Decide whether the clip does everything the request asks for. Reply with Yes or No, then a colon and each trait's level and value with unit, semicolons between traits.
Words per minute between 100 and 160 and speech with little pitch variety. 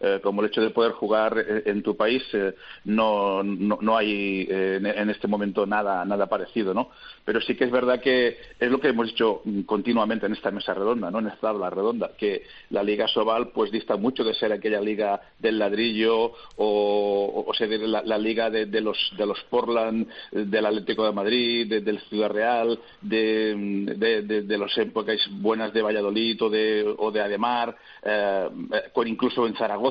No: fast, 190 wpm; narrow, 1.6 semitones